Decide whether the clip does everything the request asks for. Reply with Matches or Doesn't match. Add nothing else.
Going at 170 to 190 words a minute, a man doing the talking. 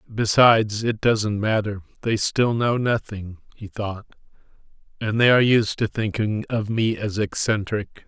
Doesn't match